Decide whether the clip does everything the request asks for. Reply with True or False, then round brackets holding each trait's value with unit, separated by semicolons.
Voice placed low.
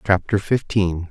True (100 Hz)